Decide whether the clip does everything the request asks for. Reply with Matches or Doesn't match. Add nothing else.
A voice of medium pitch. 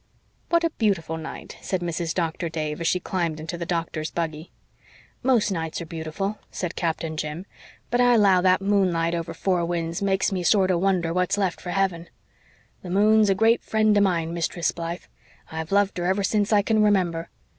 Matches